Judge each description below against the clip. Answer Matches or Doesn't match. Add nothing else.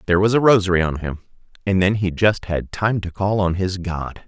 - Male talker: Matches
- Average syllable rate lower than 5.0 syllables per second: Doesn't match